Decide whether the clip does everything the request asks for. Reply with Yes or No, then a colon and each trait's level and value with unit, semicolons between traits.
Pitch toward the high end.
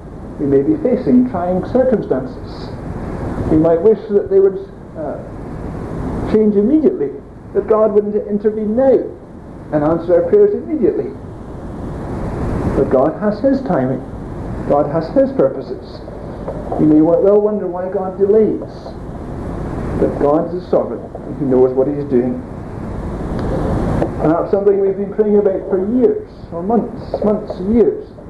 Yes: high, 200 Hz